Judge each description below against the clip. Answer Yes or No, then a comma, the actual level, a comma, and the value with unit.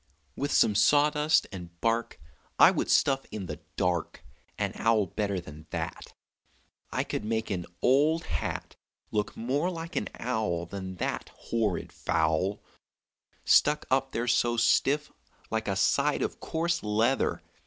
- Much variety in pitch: Yes, wide, 6.1 semitones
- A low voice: Yes, low, 110 Hz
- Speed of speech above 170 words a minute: No, average, 145 wpm